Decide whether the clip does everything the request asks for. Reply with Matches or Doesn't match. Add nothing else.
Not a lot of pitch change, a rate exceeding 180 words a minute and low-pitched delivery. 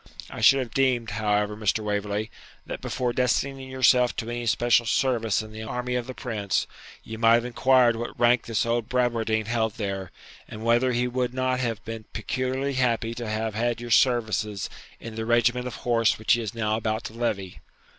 Matches